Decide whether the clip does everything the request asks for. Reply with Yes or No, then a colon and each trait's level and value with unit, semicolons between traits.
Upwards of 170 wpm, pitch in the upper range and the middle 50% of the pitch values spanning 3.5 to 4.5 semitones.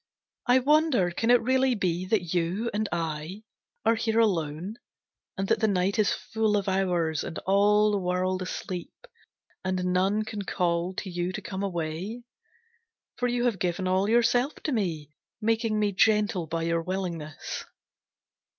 No: average, 160 wpm; high, 195 Hz; average, 3.9 semitones